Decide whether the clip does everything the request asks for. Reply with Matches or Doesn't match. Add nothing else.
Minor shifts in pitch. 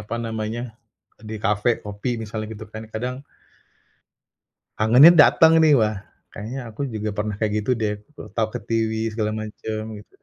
Matches